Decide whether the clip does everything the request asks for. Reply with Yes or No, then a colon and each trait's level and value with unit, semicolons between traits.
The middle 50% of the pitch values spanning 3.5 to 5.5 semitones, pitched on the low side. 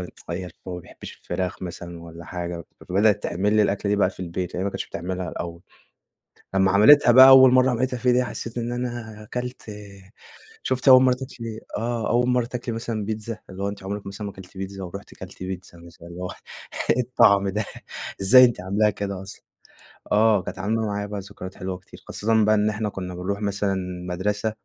Yes: average, 3.8 semitones; low, 100 Hz